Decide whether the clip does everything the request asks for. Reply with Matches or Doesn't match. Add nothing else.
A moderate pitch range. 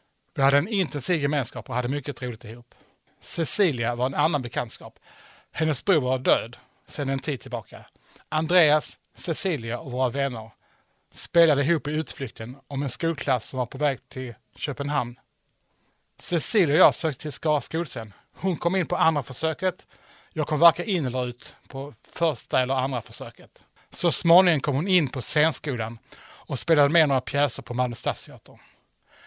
Matches